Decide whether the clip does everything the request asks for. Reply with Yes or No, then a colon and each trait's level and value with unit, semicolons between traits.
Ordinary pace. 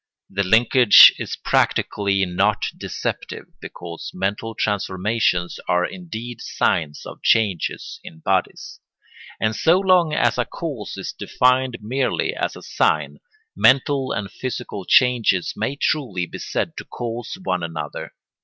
No: slow, 130 wpm